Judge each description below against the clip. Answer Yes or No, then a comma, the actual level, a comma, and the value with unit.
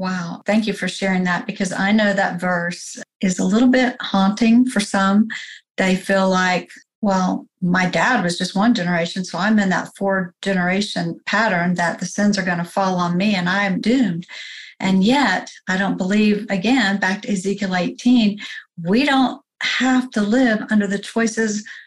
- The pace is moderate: Yes, average, 180 wpm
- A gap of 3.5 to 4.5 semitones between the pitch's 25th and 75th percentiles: No, average, 3.1 semitones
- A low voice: No, high, 200 Hz